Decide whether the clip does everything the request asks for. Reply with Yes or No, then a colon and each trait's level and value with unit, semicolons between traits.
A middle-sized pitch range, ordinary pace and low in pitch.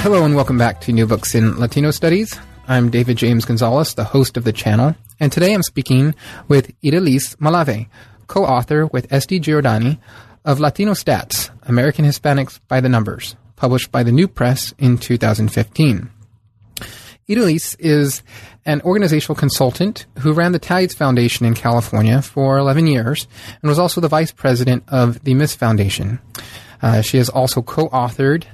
Yes: average, 4.4 semitones; average, 160 wpm; low, 130 Hz